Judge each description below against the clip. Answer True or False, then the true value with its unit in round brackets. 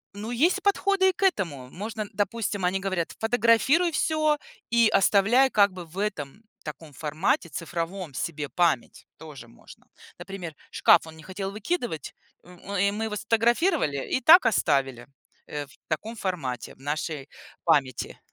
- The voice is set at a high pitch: True (195 Hz)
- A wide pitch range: True (6.8 semitones)